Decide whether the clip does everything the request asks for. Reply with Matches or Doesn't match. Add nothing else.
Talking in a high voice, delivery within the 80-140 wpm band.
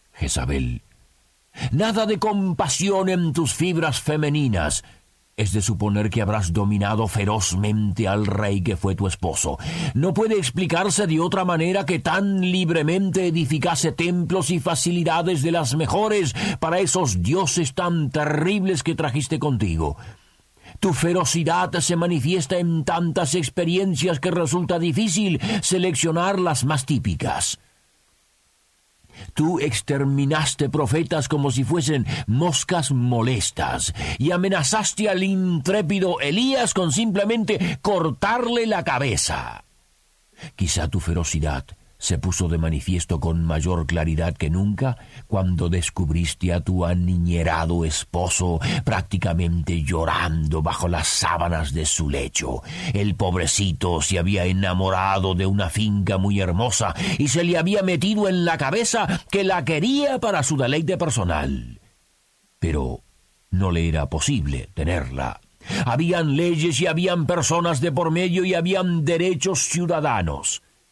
Doesn't match